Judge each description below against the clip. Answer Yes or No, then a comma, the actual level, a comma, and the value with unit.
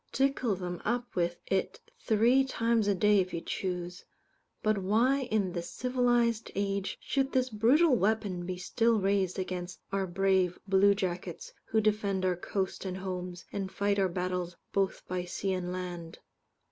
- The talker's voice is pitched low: No, high, 195 Hz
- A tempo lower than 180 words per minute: Yes, average, 160 wpm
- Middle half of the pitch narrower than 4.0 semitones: Yes, average, 3.4 semitones